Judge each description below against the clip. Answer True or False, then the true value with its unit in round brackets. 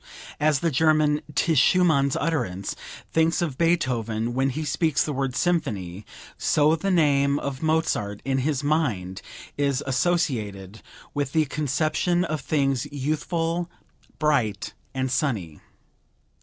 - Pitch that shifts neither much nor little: True (3.9 semitones)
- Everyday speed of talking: False (125 wpm)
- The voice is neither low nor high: True (145 Hz)